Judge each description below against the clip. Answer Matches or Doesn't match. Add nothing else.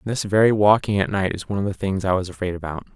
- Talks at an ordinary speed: Doesn't match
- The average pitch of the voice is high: Doesn't match